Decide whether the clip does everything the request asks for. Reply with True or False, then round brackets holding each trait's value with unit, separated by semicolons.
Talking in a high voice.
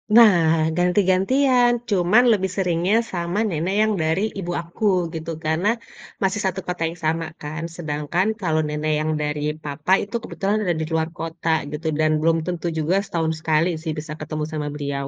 False (170 Hz)